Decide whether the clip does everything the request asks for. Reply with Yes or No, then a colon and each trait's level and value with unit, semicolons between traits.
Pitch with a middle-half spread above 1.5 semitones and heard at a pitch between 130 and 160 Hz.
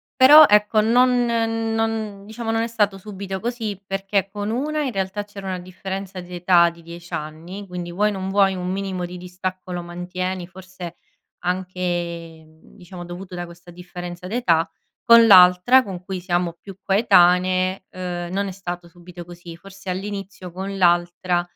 No: narrow, 2.5 semitones; medium, 185 Hz